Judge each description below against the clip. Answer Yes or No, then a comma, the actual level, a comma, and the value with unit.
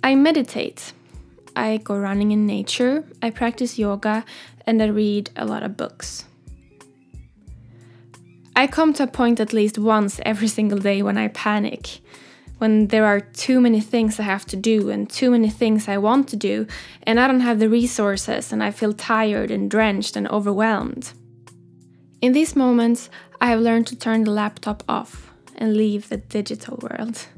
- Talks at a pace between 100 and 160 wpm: No, average, 175 wpm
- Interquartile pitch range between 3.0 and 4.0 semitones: No, narrow, 2.4 semitones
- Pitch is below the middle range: No, high, 220 Hz